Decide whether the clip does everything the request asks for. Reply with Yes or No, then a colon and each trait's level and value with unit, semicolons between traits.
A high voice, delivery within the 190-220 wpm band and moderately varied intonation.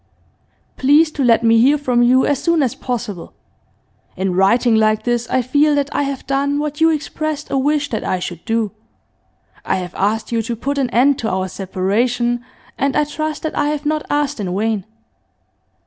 Yes: very high, 250 Hz; average, 195 wpm; average, 4.7 semitones